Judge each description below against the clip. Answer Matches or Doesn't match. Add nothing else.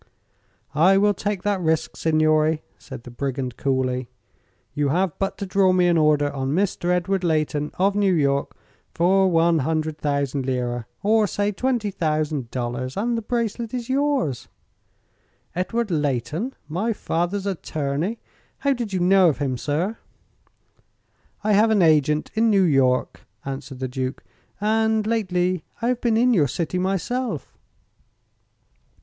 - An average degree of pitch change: Doesn't match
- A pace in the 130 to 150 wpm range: Matches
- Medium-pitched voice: Matches